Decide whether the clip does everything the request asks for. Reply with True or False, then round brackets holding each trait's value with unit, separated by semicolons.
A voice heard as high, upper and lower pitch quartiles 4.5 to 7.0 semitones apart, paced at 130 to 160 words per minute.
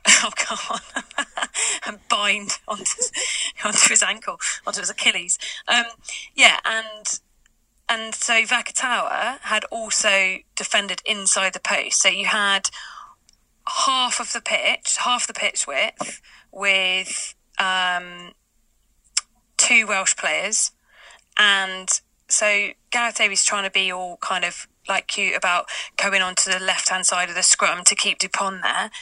False (205 Hz; 3.9 semitones; 135 wpm)